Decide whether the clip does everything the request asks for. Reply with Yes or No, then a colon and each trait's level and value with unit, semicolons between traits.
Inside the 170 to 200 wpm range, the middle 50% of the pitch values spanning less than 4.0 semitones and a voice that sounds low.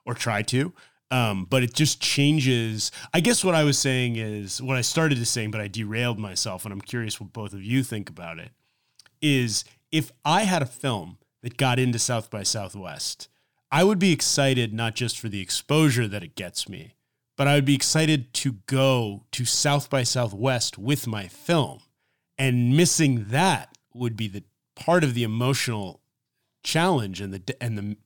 No: average, 190 wpm; average, 4.3 semitones; low, 125 Hz